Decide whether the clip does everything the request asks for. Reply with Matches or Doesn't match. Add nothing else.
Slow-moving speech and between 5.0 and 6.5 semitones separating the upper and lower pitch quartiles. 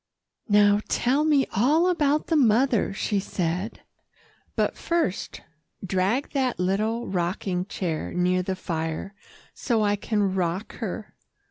Matches